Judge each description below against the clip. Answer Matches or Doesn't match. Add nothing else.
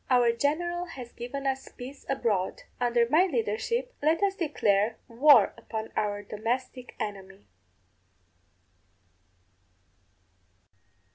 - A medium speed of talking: Doesn't match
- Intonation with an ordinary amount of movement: Matches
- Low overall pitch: Doesn't match